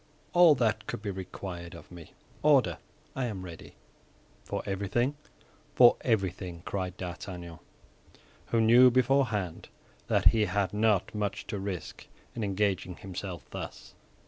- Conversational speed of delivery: No, slow, 130 wpm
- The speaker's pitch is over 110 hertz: No, low, 100 Hz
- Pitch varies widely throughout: No, average, 3.9 semitones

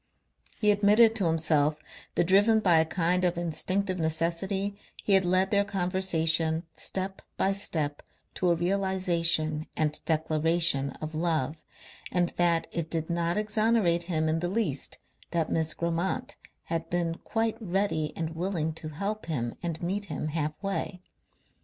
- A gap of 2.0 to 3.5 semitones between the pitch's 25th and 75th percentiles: Yes, average, 3.1 semitones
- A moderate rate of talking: Yes, average, 150 wpm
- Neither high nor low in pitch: Yes, medium, 170 Hz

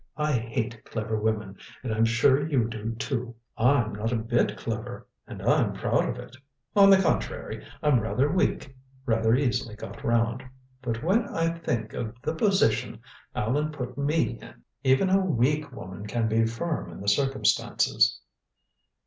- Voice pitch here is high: No, low, 120 Hz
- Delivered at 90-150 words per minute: No, average, 160 wpm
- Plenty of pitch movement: No, average, 4.6 semitones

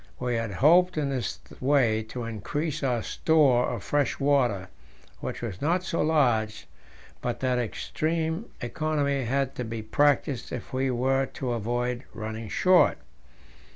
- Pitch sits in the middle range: No, low, 130 Hz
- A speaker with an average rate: Yes, average, 145 wpm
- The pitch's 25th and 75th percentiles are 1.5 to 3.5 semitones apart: No, average, 4.0 semitones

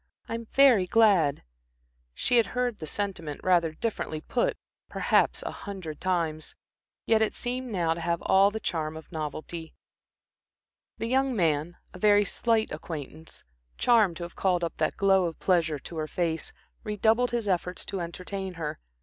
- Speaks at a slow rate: No, average, 160 wpm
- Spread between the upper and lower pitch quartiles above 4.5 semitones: Yes, average, 5.2 semitones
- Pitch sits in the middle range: Yes, medium, 180 Hz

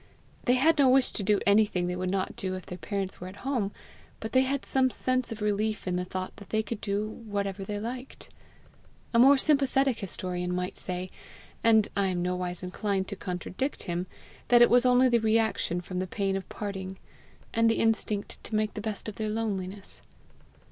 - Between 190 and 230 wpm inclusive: Yes, average, 200 wpm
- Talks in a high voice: Yes, high, 205 Hz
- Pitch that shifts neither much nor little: Yes, average, 3.8 semitones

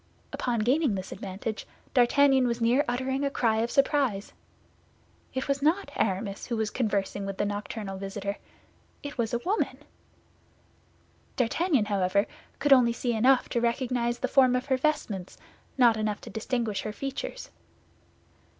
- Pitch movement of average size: Yes, average, 4.2 semitones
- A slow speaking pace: No, average, 150 wpm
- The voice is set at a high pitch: Yes, high, 235 Hz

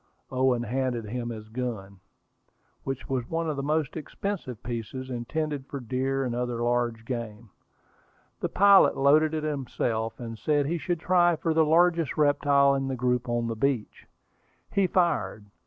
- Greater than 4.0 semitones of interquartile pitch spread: Yes, average, 4.5 semitones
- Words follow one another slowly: No, average, 160 wpm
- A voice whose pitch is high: No, low, 130 Hz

